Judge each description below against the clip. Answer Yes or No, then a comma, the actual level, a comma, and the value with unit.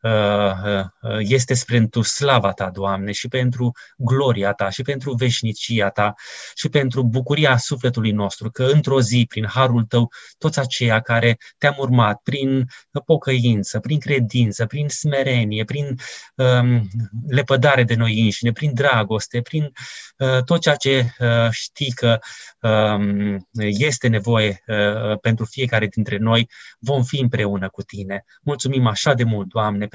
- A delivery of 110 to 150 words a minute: Yes, average, 140 wpm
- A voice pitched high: No, low, 120 Hz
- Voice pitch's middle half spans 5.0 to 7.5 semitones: No, average, 3.7 semitones